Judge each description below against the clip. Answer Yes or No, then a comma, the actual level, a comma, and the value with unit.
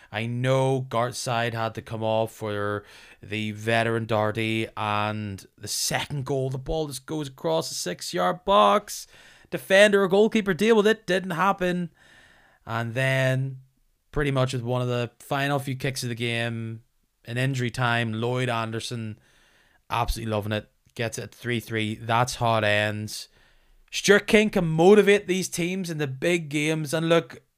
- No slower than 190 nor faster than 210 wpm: No, average, 165 wpm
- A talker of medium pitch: No, low, 125 Hz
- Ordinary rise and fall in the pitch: No, wide, 6.3 semitones